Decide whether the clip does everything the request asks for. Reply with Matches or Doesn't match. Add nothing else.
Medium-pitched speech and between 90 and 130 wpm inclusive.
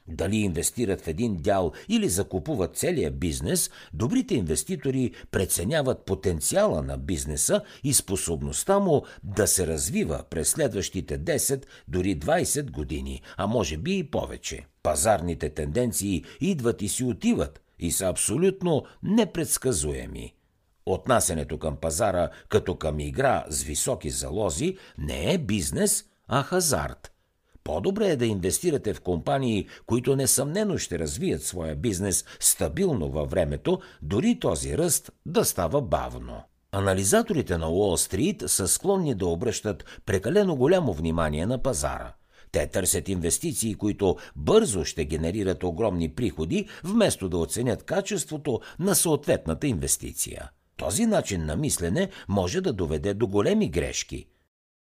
Doesn't match